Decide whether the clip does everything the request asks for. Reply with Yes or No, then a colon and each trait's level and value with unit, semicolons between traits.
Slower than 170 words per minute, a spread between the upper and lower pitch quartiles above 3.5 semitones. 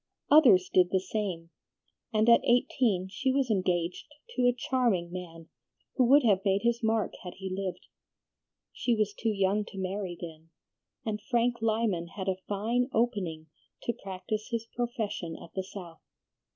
Yes: average, 160 wpm; average, 4.2 semitones